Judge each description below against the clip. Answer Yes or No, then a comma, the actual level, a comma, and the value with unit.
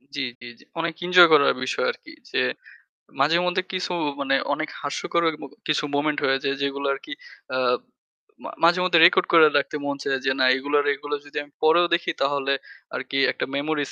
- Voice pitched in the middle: Yes, medium, 145 Hz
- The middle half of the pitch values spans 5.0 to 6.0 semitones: No, average, 3.2 semitones